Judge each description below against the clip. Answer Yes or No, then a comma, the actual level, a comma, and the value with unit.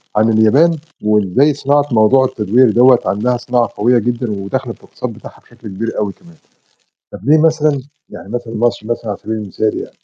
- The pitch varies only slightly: No, average, 3.7 semitones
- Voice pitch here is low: Yes, low, 120 Hz